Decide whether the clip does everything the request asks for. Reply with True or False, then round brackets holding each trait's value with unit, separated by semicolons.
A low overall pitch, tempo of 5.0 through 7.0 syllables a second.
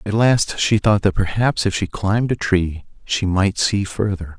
False (100 Hz; 4.4 syllables/s)